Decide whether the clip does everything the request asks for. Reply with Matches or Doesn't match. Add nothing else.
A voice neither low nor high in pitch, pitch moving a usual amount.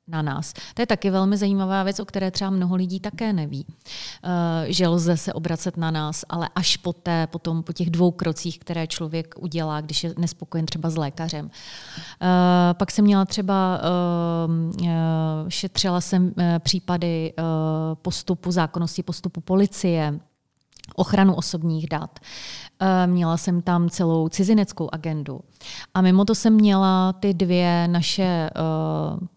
Doesn't match